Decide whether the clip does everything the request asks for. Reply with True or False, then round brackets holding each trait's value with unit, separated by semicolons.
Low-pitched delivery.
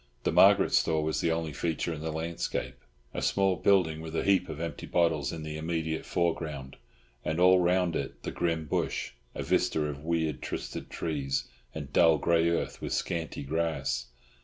True (80 Hz)